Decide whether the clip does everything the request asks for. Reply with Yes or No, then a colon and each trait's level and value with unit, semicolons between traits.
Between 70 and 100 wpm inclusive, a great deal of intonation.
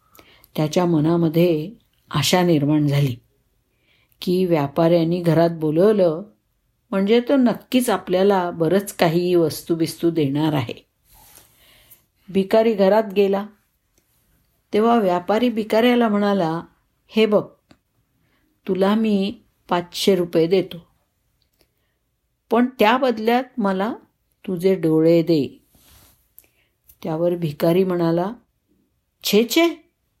No: average, 85 wpm; average, 4.3 semitones